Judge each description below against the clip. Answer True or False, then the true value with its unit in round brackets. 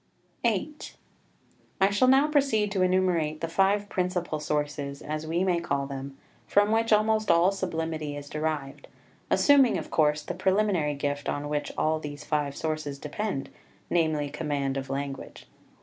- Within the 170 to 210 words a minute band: False (150 wpm)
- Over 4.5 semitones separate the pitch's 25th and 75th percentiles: True (5.1 semitones)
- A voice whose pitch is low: False (160 Hz)